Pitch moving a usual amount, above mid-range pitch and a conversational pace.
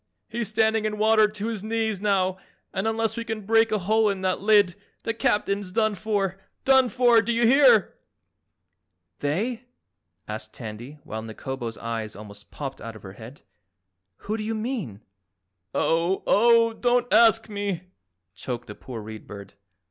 No: wide, 8.6 semitones; high, 210 Hz; average, 160 wpm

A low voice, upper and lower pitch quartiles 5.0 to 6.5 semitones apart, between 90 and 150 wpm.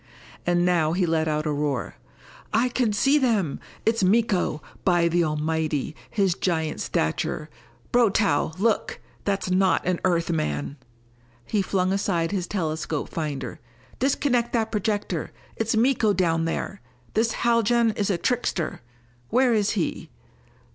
No: medium, 185 Hz; wide, 5.6 semitones; slow, 135 wpm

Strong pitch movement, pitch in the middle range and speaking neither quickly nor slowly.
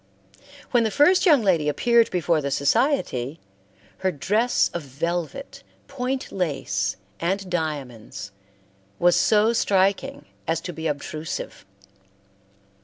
No: wide, 7.8 semitones; medium, 175 Hz; slow, 110 wpm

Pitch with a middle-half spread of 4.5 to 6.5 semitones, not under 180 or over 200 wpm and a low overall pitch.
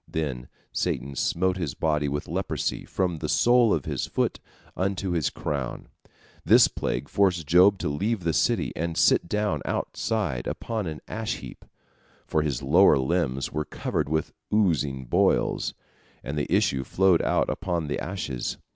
No: average, 4.9 semitones; average, 155 wpm; very low, 80 Hz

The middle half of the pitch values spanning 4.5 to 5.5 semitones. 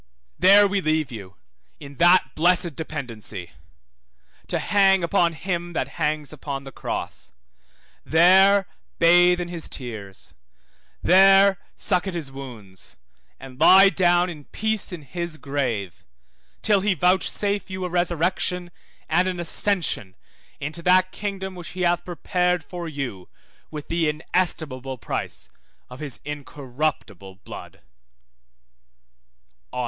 Yes: average, 4.8 semitones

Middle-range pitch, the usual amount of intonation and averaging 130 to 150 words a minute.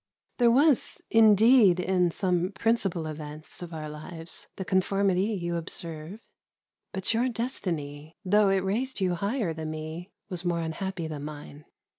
Yes: medium, 180 Hz; average, 4.2 semitones; average, 145 wpm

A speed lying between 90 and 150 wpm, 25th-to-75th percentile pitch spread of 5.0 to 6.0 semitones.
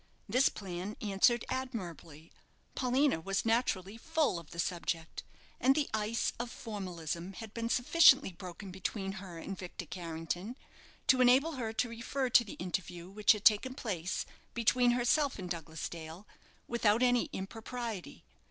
Yes: average, 145 wpm; wide, 5.5 semitones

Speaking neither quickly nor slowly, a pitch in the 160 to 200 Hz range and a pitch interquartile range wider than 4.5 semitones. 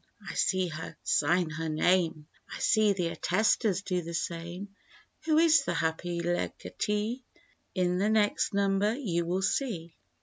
No: average, 145 wpm; medium, 185 Hz; average, 3.5 semitones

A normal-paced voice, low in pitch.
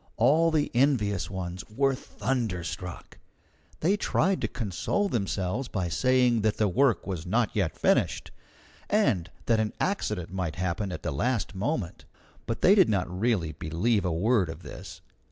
Yes: average, 155 wpm; low, 105 Hz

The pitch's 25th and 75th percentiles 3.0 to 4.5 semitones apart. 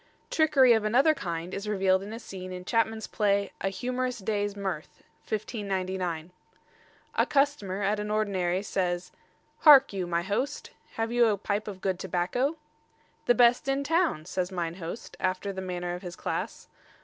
Yes: average, 4.0 semitones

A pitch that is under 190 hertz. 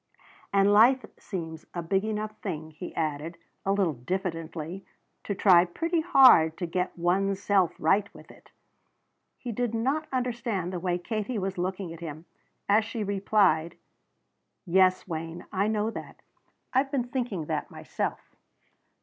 No: high, 195 Hz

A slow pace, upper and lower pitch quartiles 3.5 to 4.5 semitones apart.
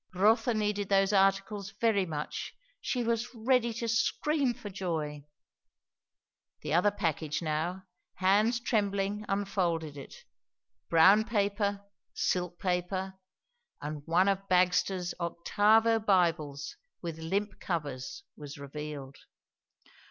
Yes: slow, 105 wpm; average, 4.1 semitones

